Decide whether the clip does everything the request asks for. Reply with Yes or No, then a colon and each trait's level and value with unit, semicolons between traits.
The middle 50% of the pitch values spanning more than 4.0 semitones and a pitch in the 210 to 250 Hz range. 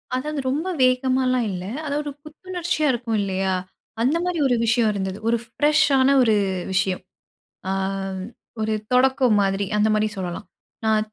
Yes: average, 5.1 semitones; high, 245 Hz